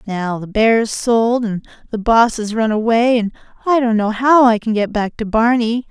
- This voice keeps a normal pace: No, fast, 215 wpm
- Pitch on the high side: Yes, high, 225 Hz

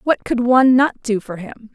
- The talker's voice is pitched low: No, high, 240 Hz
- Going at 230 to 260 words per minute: Yes, fast, 240 wpm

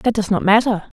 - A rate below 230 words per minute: No, fast, 245 wpm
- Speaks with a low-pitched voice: No, high, 210 Hz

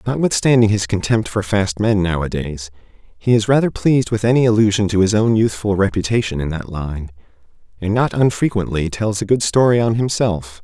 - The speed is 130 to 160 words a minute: No, average, 175 wpm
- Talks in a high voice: No, low, 105 Hz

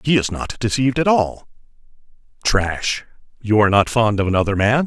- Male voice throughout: Yes, male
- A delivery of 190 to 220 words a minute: No, average, 160 wpm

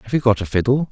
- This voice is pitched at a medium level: No, low, 120 Hz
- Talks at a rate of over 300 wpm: Yes, fast, 330 wpm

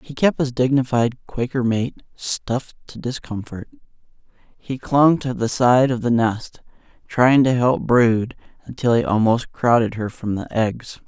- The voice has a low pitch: Yes, low, 120 Hz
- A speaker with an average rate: Yes, average, 155 wpm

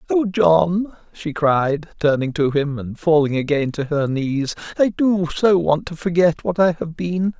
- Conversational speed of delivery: Yes, average, 185 wpm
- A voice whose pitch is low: No, medium, 165 Hz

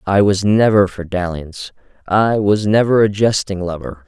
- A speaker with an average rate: Yes, average, 160 wpm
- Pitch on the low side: Yes, low, 100 Hz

